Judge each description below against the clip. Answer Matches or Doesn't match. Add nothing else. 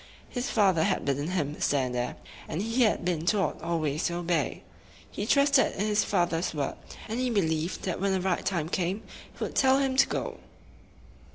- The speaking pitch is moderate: Matches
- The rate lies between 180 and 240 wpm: Matches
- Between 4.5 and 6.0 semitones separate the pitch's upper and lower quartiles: Matches